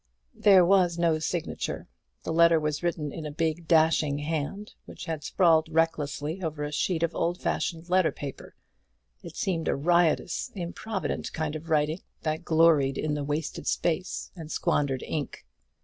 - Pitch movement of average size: No, narrow, 2.2 semitones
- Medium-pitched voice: Yes, medium, 160 Hz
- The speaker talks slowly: No, average, 160 wpm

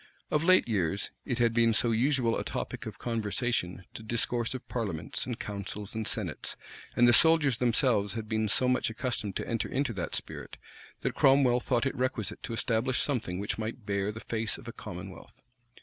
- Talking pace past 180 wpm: Yes, average, 190 wpm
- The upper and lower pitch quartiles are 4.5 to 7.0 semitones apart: No, average, 2.9 semitones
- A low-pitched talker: Yes, low, 115 Hz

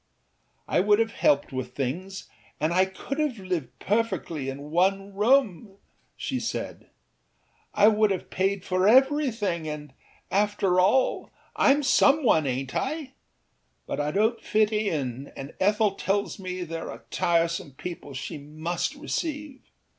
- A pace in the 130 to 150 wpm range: Yes, slow, 135 wpm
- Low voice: No, high, 195 Hz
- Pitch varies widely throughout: Yes, wide, 5.7 semitones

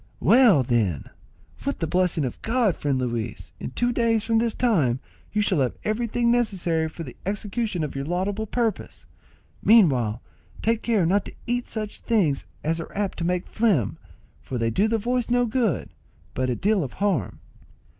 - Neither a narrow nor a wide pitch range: No, wide, 8.0 semitones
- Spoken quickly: No, average, 175 wpm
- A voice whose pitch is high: Yes, high, 195 Hz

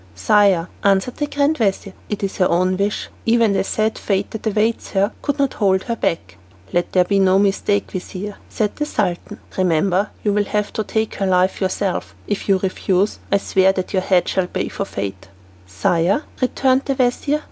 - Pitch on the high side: Yes, high, 200 Hz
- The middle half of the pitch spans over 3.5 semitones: No, narrow, 2.6 semitones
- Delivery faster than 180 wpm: Yes, average, 190 wpm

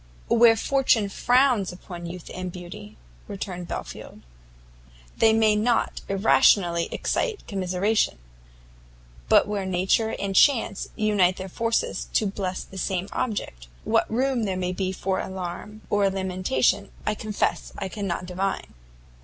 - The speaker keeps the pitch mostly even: No, average, 3.1 semitones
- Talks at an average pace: No, slow, 130 wpm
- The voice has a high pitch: Yes, high, 195 Hz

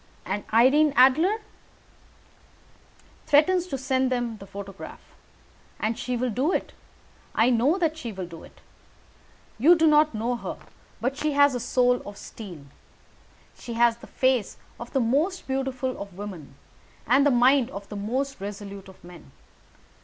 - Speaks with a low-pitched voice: No, high, 245 Hz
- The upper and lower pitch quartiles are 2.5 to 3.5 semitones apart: No, average, 5.1 semitones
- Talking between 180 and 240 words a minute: No, average, 155 wpm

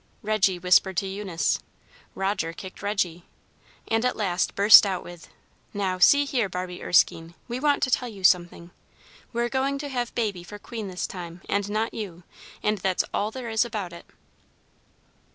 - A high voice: Yes, high, 200 Hz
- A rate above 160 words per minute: Yes, average, 170 wpm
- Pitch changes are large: No, average, 4.0 semitones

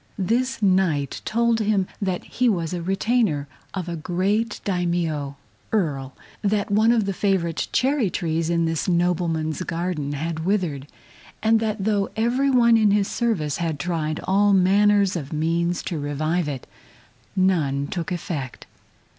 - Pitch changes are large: No, average, 4.5 semitones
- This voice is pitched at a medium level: Yes, medium, 180 Hz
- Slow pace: No, average, 145 wpm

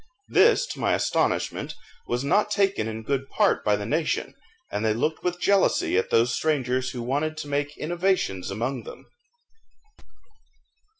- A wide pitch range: Yes, wide, 6.5 semitones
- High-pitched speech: No, medium, 140 Hz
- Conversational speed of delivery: Yes, average, 155 wpm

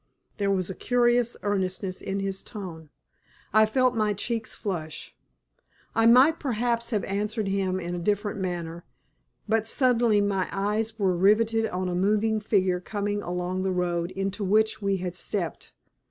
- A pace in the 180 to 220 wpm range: No, average, 155 wpm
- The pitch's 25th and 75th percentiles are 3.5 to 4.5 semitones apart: No, average, 3.0 semitones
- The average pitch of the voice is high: Yes, high, 200 Hz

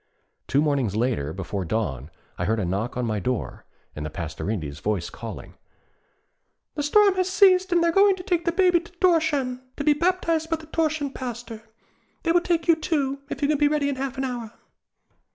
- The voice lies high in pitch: Yes, very high, 280 Hz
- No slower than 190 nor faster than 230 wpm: Yes, fast, 205 wpm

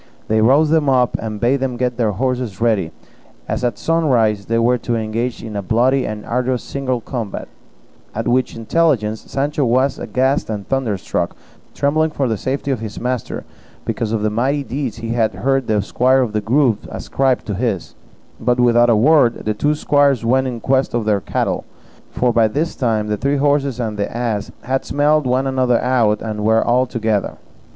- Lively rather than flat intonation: No, average, 3.4 semitones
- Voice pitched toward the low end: Yes, low, 120 Hz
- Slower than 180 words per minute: No, average, 190 wpm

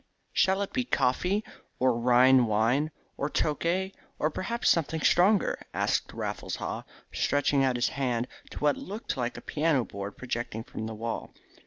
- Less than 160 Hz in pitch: Yes, medium, 140 Hz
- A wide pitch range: Yes, wide, 5.9 semitones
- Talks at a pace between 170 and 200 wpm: No, average, 160 wpm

